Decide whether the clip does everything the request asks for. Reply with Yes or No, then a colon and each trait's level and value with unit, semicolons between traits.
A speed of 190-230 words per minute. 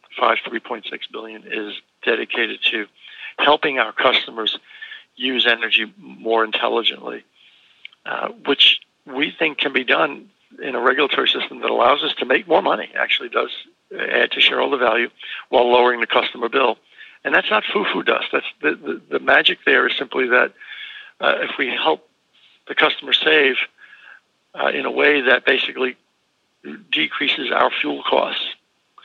No: average, 150 wpm